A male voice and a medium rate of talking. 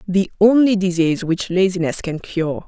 No: female; average, 155 wpm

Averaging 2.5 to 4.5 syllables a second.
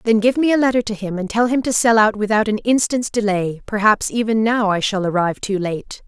No: 5.6 syllables/s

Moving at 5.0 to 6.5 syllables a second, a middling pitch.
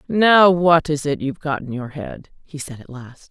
No: 4.6 syllables/s; medium, 150 Hz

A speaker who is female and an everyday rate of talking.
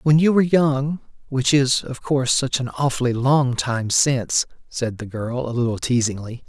No: male; average, 175 wpm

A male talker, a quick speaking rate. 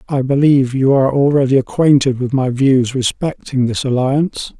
No: male; average, 155 wpm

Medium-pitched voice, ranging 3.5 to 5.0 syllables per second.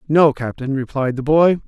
Yes: medium, 145 Hz; 4.8 syllables/s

